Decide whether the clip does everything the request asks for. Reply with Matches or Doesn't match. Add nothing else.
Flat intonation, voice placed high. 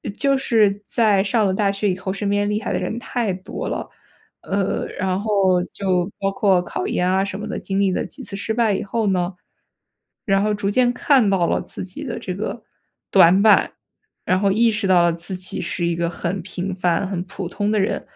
Matches